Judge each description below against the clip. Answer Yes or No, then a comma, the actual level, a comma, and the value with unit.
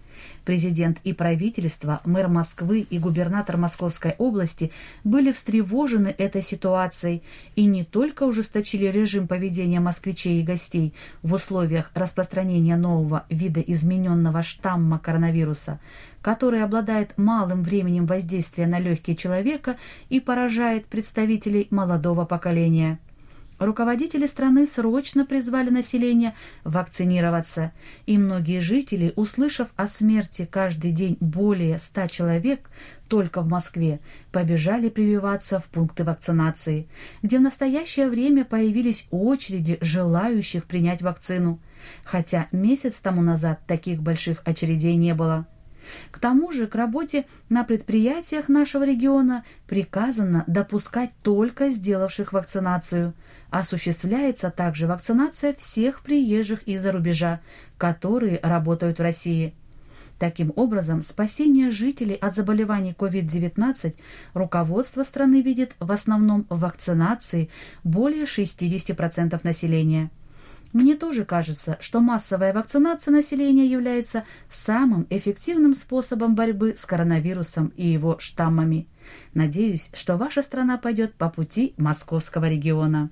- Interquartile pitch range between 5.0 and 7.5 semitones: Yes, average, 5.3 semitones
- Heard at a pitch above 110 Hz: Yes, medium, 185 Hz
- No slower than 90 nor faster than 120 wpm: Yes, slow, 110 wpm